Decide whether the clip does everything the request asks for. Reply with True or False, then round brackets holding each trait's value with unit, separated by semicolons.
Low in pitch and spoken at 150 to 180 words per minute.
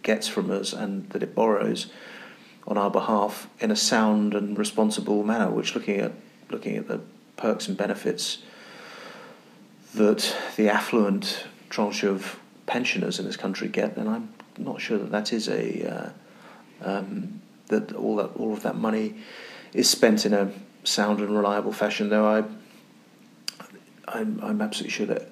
True (110 Hz; 160 wpm)